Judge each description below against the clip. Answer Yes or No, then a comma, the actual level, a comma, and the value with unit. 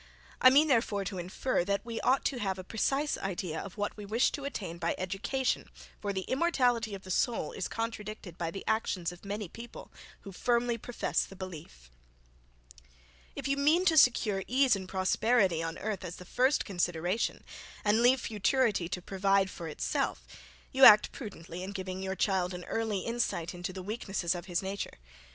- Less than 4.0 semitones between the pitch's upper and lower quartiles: No, average, 4.4 semitones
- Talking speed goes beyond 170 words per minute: Yes, average, 180 wpm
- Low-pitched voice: No, high, 200 Hz